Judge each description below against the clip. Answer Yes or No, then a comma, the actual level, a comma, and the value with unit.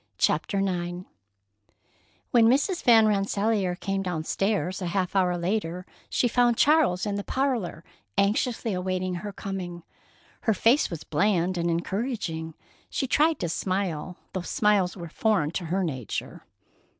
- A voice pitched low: No, high, 190 Hz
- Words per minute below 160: Yes, average, 140 wpm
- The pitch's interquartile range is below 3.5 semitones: No, average, 3.8 semitones